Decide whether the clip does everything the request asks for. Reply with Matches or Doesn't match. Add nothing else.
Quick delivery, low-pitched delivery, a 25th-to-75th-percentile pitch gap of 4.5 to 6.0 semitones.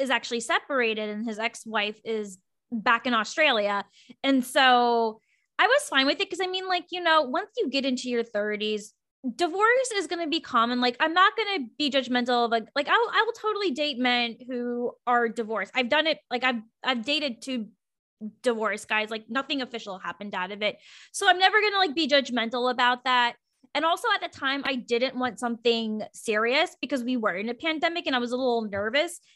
Doesn't match